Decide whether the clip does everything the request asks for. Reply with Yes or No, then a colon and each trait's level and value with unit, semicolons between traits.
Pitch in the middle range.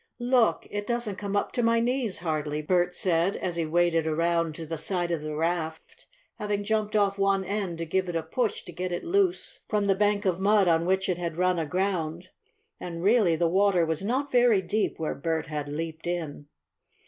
Yes: medium, 180 Hz